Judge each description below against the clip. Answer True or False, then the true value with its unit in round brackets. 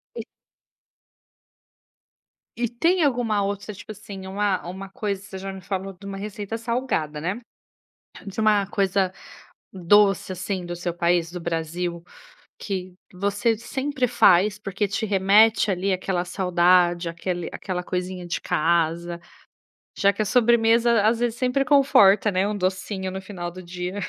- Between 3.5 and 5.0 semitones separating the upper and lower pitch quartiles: False (2.9 semitones)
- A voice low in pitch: False (195 Hz)